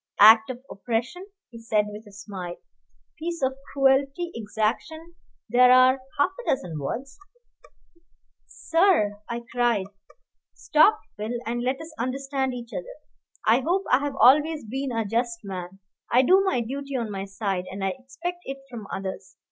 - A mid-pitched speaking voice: No, high, 245 Hz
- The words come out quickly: No, average, 165 wpm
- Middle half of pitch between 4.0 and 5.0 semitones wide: Yes, average, 4.7 semitones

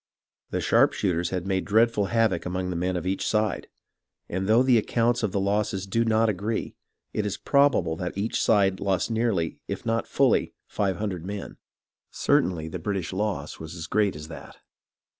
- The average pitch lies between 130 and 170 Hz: No, low, 100 Hz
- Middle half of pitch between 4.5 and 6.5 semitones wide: No, average, 3.1 semitones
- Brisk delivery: No, average, 180 wpm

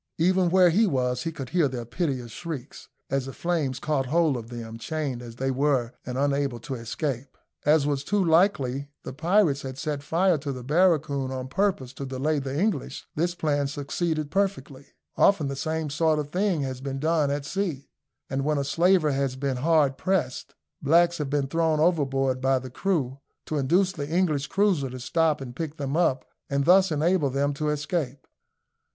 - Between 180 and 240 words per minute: Yes, average, 190 wpm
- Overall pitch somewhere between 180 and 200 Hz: No, medium, 145 Hz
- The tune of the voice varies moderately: Yes, average, 3.7 semitones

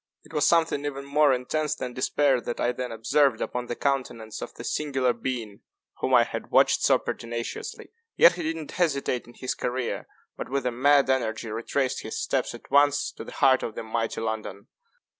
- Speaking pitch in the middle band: No, low, 130 Hz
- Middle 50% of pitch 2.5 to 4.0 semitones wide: Yes, average, 3.4 semitones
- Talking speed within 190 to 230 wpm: Yes, average, 195 wpm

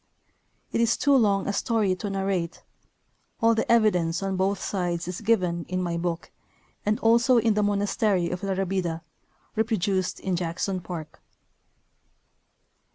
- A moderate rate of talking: Yes, average, 145 wpm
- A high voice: Yes, high, 195 Hz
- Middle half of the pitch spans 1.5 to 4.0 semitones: Yes, average, 3.3 semitones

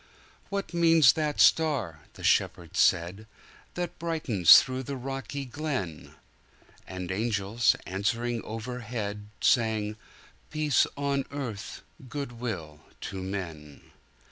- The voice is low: Yes, low, 115 Hz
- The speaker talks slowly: Yes, slow, 90 wpm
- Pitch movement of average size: No, wide, 6.0 semitones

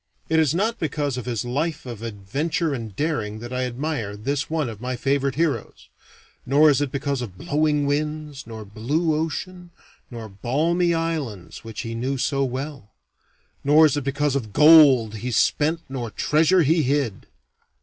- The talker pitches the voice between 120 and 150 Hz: Yes, medium, 140 Hz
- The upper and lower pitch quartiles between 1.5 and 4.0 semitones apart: No, average, 4.5 semitones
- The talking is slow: No, average, 170 wpm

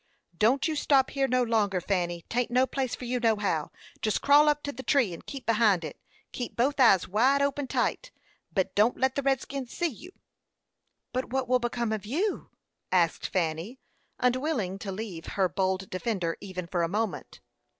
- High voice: Yes, high, 235 Hz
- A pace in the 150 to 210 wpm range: Yes, average, 180 wpm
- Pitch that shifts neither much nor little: No, wide, 5.7 semitones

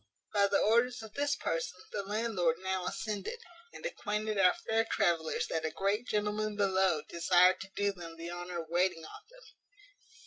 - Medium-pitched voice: No, high, 195 Hz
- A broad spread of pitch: No, average, 3.4 semitones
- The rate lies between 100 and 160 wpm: No, average, 175 wpm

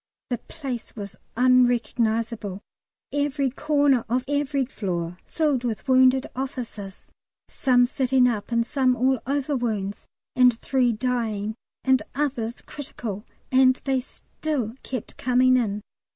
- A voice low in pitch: No, very high, 250 Hz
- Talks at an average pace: No, slow, 125 wpm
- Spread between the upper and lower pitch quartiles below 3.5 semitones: Yes, average, 2.7 semitones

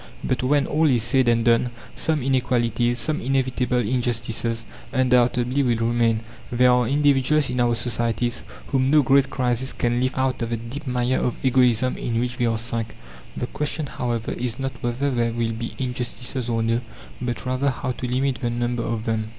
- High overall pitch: No, low, 125 Hz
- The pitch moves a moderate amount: No, narrow, 1.9 semitones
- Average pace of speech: Yes, average, 185 wpm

